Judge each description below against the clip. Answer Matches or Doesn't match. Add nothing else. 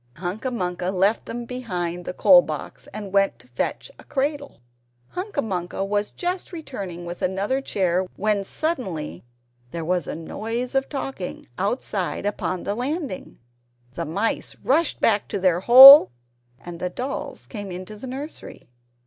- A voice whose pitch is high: Matches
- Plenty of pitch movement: Matches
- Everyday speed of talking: Matches